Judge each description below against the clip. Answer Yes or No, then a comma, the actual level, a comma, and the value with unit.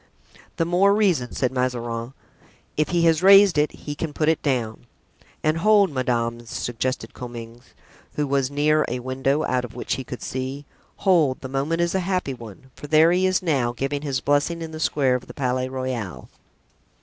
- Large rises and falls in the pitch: No, average, 4.4 semitones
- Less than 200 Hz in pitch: Yes, medium, 140 Hz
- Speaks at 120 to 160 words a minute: No, average, 185 wpm